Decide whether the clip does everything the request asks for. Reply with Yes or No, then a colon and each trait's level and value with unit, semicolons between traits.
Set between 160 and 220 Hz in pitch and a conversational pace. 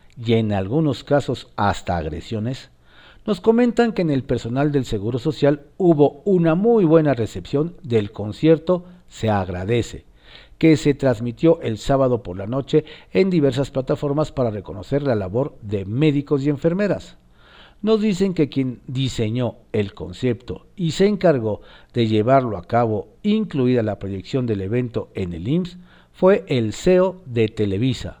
No: low, 130 Hz; average, 150 wpm